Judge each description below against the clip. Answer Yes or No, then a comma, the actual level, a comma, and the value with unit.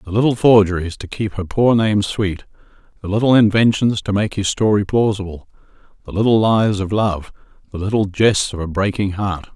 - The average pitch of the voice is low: Yes, low, 100 Hz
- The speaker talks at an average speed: Yes, average, 180 wpm